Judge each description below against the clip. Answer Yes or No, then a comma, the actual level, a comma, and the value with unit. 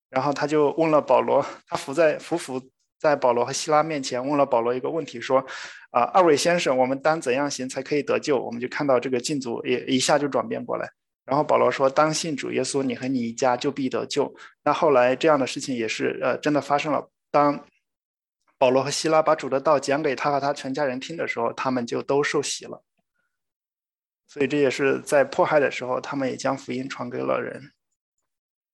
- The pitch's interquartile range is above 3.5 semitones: No, average, 2.7 semitones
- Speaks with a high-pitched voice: No, medium, 140 Hz